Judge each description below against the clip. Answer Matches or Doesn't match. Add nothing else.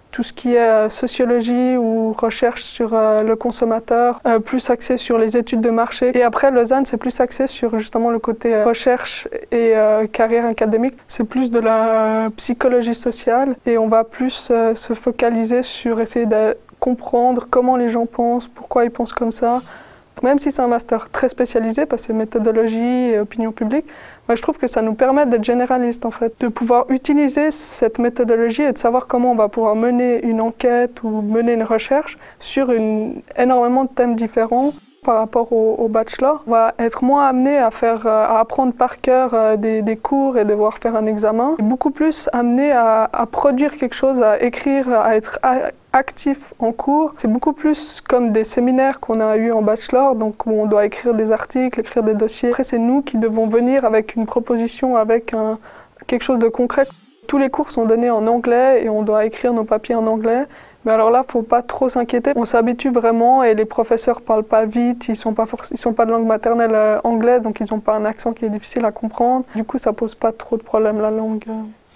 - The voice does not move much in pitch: Matches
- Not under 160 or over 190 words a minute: Doesn't match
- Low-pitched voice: Doesn't match